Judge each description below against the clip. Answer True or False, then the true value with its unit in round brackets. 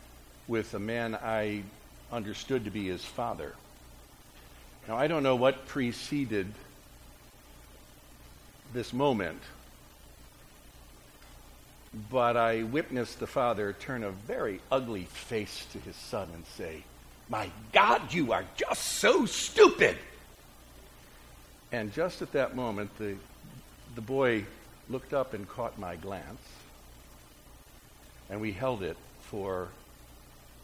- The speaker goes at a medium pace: False (115 wpm)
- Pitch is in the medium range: False (75 Hz)